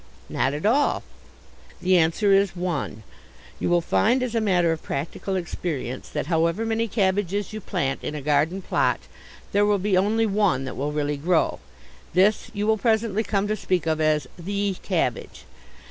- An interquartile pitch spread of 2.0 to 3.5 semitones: No, average, 4.7 semitones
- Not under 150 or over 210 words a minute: Yes, average, 175 wpm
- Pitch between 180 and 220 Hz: Yes, medium, 185 Hz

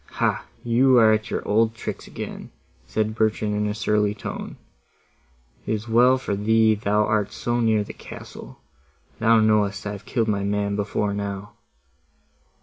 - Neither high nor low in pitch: No, low, 105 Hz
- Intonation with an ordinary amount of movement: No, narrow, 1.5 semitones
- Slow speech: No, average, 160 wpm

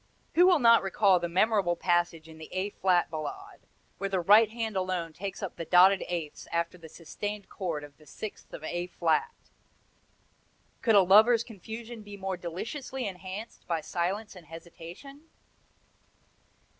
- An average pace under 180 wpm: Yes, average, 155 wpm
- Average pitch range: Yes, average, 4.1 semitones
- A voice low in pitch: No, medium, 185 Hz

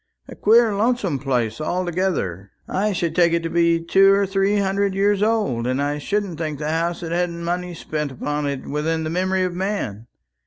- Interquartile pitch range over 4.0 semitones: Yes, average, 4.5 semitones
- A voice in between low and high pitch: Yes, medium, 170 Hz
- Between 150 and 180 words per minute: No, average, 195 wpm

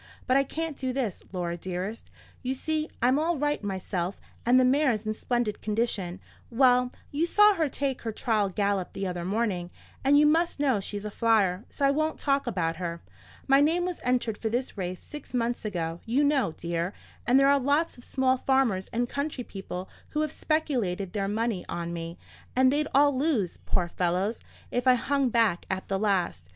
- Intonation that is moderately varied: No, wide, 6.5 semitones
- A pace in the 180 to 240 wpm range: Yes, average, 190 wpm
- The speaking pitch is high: Yes, high, 235 Hz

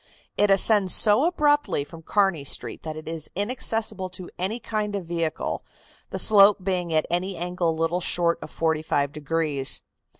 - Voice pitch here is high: No, medium, 180 Hz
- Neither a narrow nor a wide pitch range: Yes, average, 4.0 semitones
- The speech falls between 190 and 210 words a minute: No, average, 165 wpm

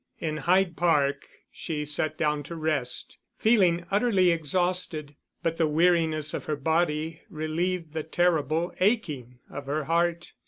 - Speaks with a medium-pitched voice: Yes, medium, 160 Hz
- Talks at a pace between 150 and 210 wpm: No, slow, 135 wpm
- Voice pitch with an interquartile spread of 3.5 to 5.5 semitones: No, narrow, 2.6 semitones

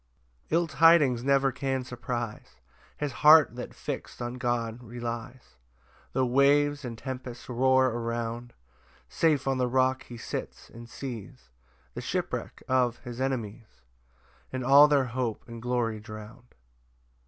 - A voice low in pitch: Yes, low, 125 Hz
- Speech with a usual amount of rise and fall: No, narrow, 2.2 semitones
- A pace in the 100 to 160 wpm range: Yes, slow, 135 wpm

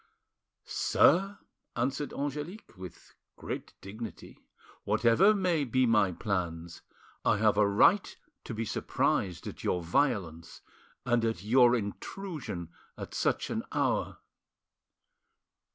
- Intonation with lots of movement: Yes, wide, 6.6 semitones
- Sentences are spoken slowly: Yes, slow, 110 wpm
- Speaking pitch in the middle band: No, low, 115 Hz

